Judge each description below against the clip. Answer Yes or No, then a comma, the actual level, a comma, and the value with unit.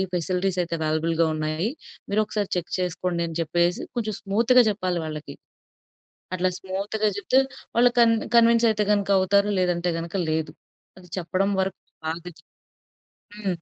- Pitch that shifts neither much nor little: Yes, average, 3.6 semitones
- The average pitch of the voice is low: No, medium, 185 Hz